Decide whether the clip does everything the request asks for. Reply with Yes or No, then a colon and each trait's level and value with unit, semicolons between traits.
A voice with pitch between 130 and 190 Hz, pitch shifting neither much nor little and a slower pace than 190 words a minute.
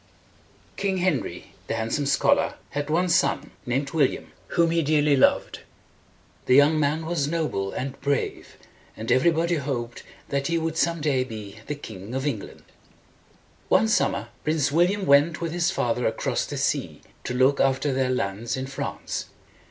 Yes: medium, 140 Hz; average, 4.2 semitones; average, 160 wpm